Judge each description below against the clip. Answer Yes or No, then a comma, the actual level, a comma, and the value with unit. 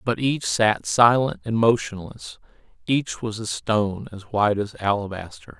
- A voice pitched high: No, low, 110 Hz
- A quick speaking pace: No, average, 140 wpm